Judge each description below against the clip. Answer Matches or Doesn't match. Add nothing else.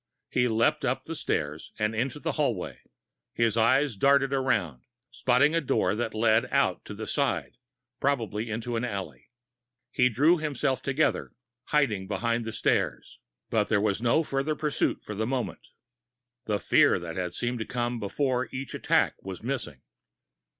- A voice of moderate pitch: Doesn't match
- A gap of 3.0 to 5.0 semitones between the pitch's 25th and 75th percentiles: Matches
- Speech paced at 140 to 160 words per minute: Matches